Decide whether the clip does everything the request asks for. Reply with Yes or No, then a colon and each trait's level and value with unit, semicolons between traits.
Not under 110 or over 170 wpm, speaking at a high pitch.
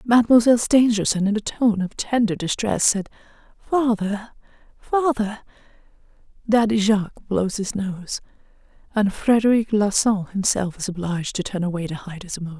Yes: slow, 135 wpm; high, 210 Hz